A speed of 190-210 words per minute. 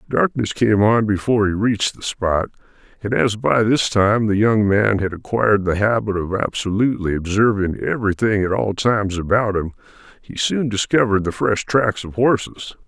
No: average, 170 wpm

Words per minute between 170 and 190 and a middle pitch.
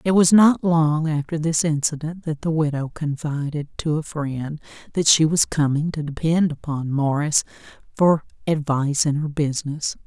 No: average, 160 wpm; medium, 155 Hz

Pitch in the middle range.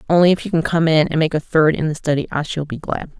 Yes: medium, 160 Hz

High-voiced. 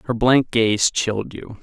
No: low, 115 Hz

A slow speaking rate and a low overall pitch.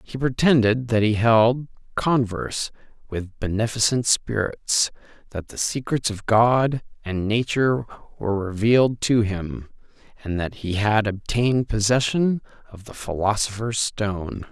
Yes: slow, 125 wpm; low, 110 Hz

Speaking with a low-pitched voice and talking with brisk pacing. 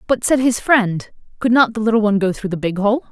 No: high, 220 Hz; fast, 270 wpm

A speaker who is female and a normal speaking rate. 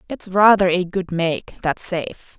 Yes: female; average, 175 wpm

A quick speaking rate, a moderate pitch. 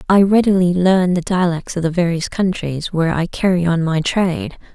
No: average, 190 wpm; medium, 175 Hz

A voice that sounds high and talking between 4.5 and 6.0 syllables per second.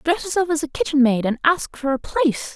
Yes: very high, 285 Hz; 5.8 syllables/s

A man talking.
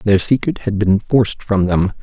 Yes: male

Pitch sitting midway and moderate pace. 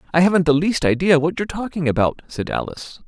No: medium, 160 Hz; fast, 215 wpm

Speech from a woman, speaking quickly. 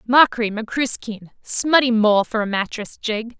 No: female; average, 140 wpm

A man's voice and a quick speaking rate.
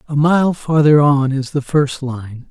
No: male; average, 190 wpm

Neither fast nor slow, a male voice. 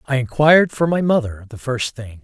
No: fast, 215 wpm; male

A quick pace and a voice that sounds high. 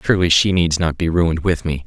No: fast, 260 wpm; very low, 85 Hz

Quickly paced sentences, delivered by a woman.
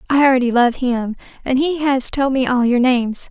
Yes: fast, 220 wpm; female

